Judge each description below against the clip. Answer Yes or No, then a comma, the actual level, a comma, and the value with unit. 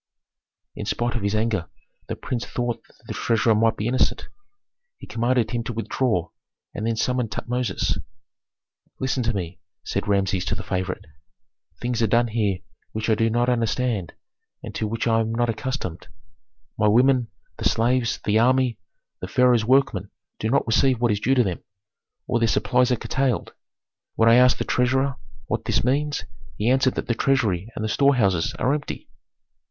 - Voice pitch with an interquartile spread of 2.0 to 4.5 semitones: Yes, average, 2.8 semitones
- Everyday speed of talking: Yes, average, 175 wpm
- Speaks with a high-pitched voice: No, low, 115 Hz